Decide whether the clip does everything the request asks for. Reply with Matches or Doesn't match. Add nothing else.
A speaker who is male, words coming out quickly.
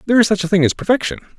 Matches